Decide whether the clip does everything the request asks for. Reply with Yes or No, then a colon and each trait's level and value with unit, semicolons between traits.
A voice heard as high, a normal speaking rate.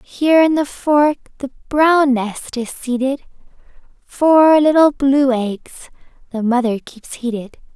No: very high, 270 Hz; slow, 130 wpm